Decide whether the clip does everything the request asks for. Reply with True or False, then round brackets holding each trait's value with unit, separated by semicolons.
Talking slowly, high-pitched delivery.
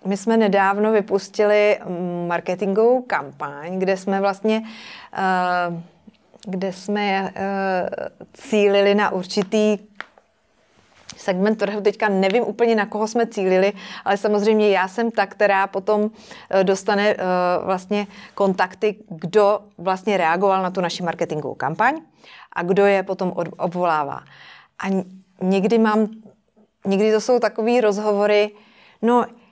True (110 wpm; 200 Hz)